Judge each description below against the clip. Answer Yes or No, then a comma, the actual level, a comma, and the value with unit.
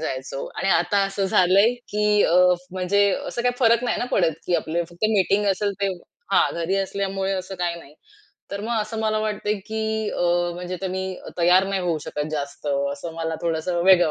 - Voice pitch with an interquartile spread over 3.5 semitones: No, average, 3.2 semitones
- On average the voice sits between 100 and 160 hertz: No, high, 190 Hz